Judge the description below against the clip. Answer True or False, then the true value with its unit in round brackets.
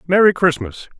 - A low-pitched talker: False (165 Hz)